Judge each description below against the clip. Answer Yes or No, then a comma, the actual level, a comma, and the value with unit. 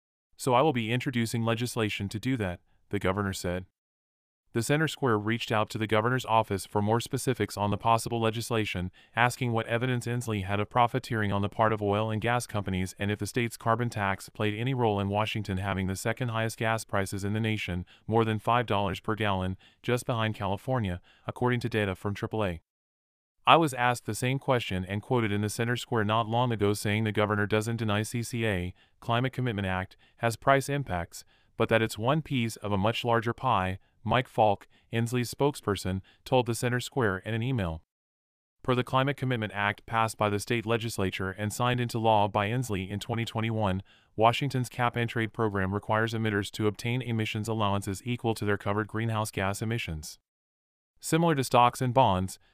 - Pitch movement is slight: No, average, 3.0 semitones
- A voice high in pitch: No, low, 110 Hz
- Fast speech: No, average, 190 wpm